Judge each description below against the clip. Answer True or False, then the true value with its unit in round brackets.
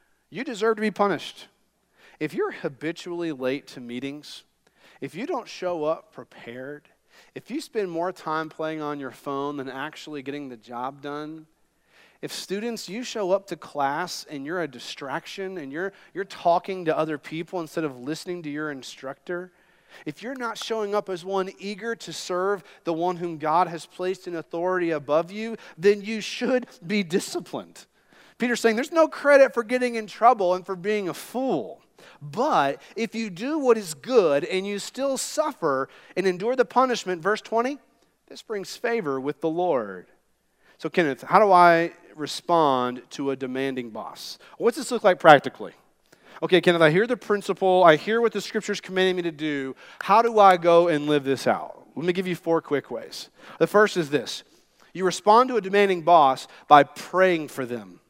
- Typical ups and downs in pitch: False (5.9 semitones)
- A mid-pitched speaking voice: True (180 Hz)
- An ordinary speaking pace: True (185 wpm)